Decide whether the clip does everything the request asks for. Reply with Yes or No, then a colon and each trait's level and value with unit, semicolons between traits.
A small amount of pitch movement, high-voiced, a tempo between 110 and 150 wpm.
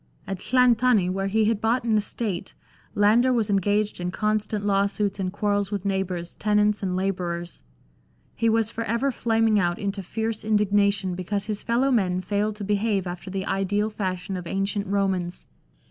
No: narrow, 2.1 semitones; high, 205 Hz; average, 170 wpm